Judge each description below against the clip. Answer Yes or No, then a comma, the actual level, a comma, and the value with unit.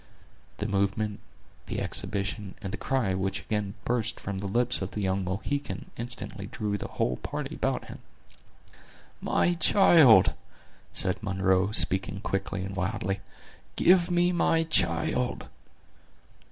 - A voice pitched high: No, low, 100 Hz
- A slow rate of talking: Yes, slow, 130 wpm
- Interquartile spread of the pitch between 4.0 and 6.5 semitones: Yes, average, 4.3 semitones